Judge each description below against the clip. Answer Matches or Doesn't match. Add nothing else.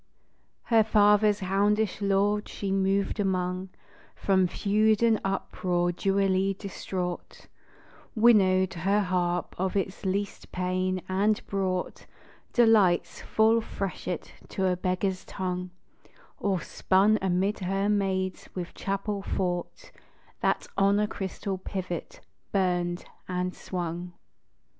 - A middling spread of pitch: Doesn't match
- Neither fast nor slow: Doesn't match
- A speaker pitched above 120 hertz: Matches